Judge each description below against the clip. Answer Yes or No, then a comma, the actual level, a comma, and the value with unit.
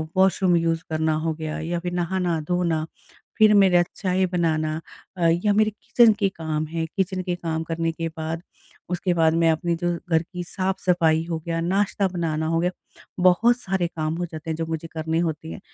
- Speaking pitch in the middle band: Yes, medium, 170 Hz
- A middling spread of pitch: No, narrow, 2.2 semitones